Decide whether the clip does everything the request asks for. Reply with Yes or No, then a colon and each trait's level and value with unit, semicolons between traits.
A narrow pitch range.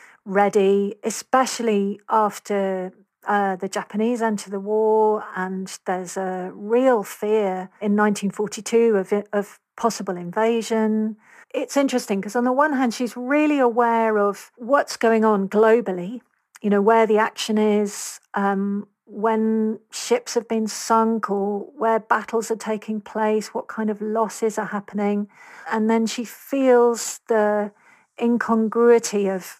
Yes: narrow, 2.0 semitones